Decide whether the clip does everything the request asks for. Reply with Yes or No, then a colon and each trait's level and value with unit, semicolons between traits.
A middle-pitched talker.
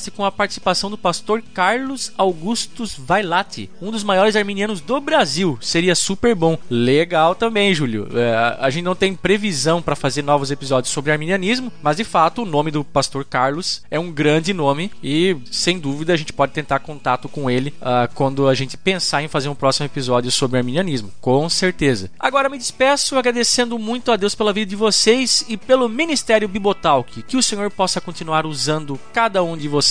Yes: medium, 175 Hz